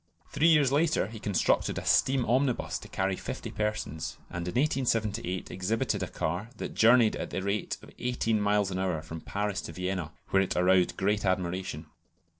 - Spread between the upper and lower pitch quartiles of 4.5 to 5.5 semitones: No, average, 3.9 semitones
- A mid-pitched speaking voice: No, low, 100 Hz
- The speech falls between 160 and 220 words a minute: Yes, average, 180 wpm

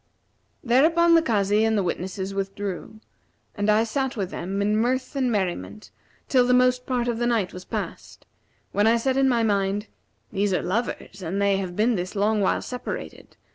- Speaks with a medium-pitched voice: No, high, 215 Hz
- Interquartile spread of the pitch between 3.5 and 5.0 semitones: Yes, average, 4.0 semitones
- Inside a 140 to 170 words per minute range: No, average, 185 wpm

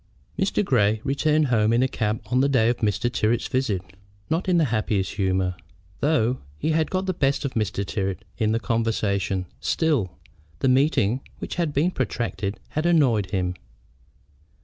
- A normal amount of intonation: No, wide, 6.0 semitones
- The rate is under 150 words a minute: No, average, 170 wpm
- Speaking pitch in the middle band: No, low, 115 Hz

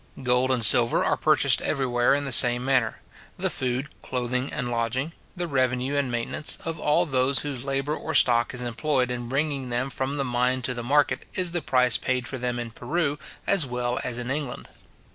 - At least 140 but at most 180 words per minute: No, average, 200 wpm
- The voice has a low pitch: Yes, low, 130 Hz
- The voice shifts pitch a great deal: No, narrow, 2.5 semitones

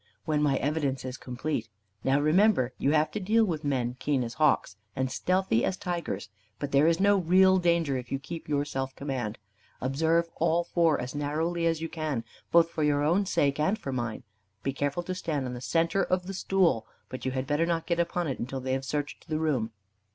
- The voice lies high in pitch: No, medium, 150 Hz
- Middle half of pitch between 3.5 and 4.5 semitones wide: Yes, average, 4.2 semitones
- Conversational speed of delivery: No, fast, 215 wpm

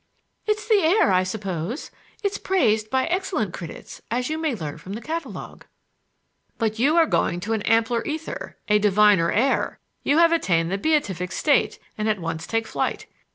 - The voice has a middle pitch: No, high, 225 Hz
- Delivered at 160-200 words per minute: Yes, average, 175 wpm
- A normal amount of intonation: No, wide, 8.4 semitones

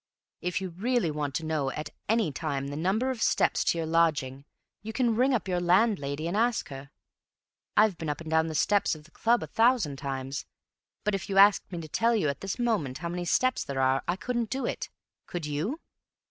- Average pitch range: No, wide, 6.8 semitones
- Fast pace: Yes, fast, 220 wpm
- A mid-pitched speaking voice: Yes, medium, 175 Hz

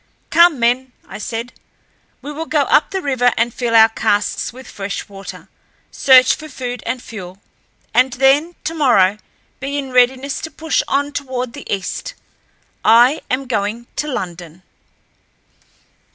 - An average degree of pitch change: Yes, average, 3.9 semitones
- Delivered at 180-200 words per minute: No, average, 145 wpm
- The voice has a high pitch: Yes, very high, 250 Hz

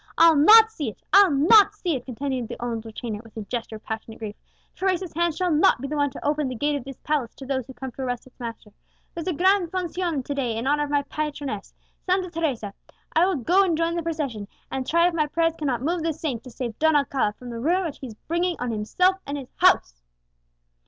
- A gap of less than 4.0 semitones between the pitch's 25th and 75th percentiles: No, wide, 5.6 semitones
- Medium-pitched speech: No, very high, 290 Hz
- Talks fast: Yes, fast, 245 wpm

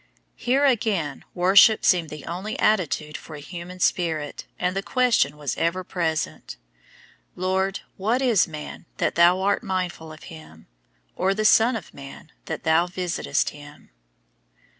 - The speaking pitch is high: No, medium, 180 Hz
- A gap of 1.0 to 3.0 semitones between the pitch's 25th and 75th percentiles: No, average, 3.8 semitones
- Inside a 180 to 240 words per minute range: No, average, 145 wpm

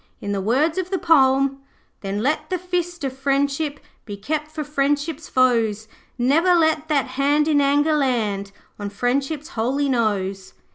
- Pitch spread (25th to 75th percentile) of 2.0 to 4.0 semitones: No, average, 4.6 semitones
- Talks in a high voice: Yes, very high, 275 Hz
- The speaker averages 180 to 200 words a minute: No, average, 155 wpm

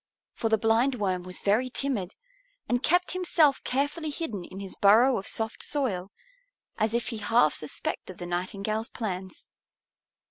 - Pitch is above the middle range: Yes, high, 220 Hz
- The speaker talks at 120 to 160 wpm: Yes, average, 145 wpm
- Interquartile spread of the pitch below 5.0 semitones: No, average, 5.3 semitones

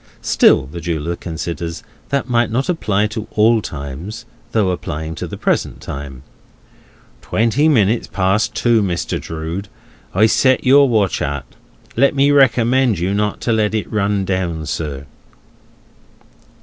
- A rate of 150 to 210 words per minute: No, average, 140 wpm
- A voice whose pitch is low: Yes, low, 105 Hz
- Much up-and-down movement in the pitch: Yes, wide, 5.8 semitones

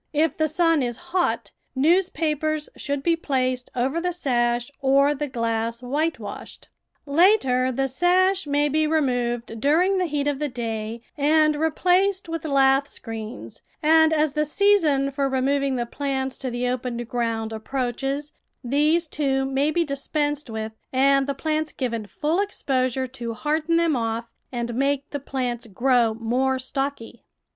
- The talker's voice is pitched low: No, very high, 275 Hz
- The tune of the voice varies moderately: Yes, average, 3.8 semitones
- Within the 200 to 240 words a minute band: No, average, 150 wpm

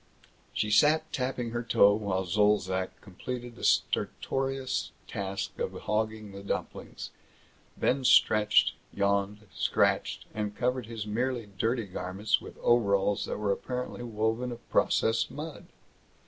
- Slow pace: Yes, slow, 125 wpm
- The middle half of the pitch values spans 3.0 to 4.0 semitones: Yes, average, 3.4 semitones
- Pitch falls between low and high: No, low, 110 Hz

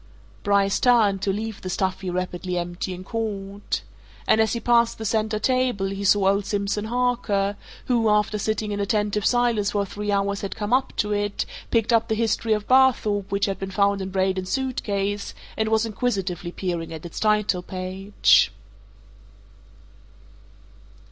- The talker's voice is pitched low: No, high, 205 Hz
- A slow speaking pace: No, average, 160 wpm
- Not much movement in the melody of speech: Yes, narrow, 2.3 semitones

